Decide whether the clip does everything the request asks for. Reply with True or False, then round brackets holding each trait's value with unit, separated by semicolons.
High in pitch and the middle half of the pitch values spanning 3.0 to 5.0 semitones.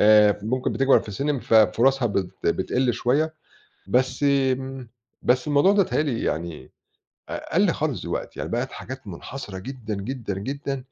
False (130 Hz; 4.4 semitones)